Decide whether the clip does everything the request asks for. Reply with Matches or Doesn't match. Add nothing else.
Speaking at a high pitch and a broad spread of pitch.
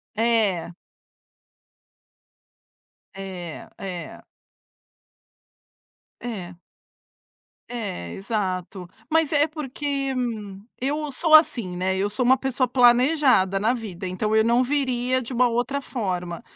Matches